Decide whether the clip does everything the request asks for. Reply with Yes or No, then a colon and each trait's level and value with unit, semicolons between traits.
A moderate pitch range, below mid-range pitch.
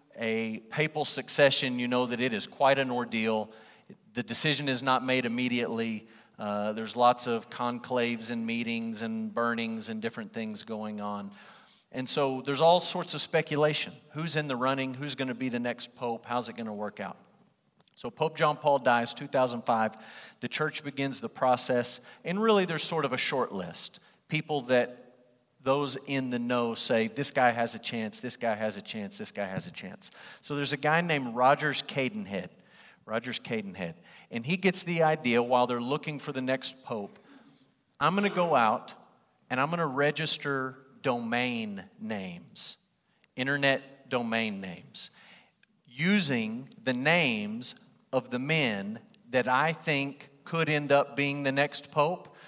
Yes: average, 4.2 semitones; low, 130 Hz